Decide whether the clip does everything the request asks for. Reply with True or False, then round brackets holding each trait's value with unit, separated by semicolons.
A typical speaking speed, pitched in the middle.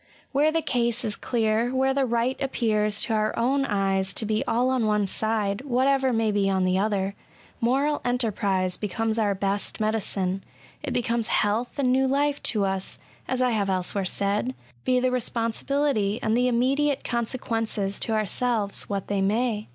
False (175 wpm; 225 Hz)